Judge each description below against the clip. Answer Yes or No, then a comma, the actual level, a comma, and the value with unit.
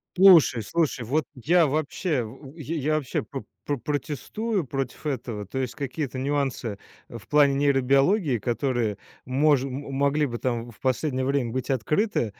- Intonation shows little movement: No, average, 3.3 semitones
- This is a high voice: No, low, 135 Hz